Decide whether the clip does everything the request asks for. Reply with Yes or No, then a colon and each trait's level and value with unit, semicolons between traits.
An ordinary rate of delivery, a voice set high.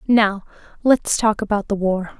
Yes: average, 165 wpm; high, 210 Hz